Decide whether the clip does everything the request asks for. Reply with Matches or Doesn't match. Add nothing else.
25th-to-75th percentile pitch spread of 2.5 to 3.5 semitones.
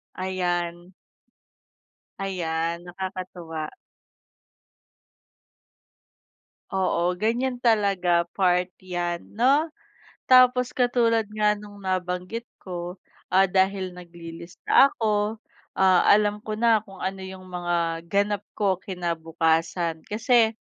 Matches